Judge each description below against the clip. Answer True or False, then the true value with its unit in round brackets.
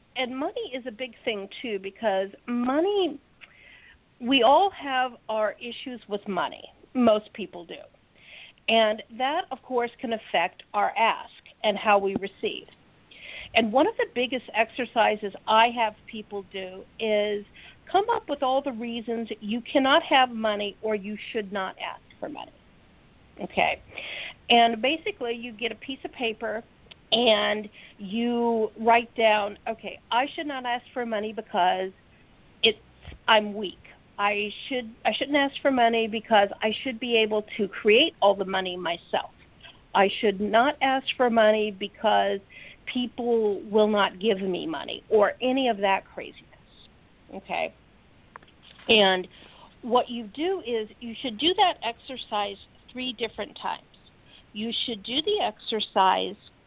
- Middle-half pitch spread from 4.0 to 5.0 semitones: False (3.6 semitones)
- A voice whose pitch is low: False (230 Hz)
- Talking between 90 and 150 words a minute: True (145 wpm)